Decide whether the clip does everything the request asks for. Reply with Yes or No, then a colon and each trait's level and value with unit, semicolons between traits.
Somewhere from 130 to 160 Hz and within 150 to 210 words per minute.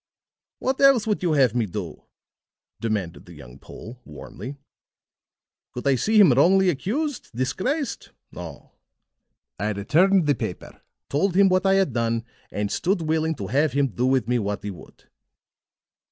Yes: low, 135 Hz; average, 155 wpm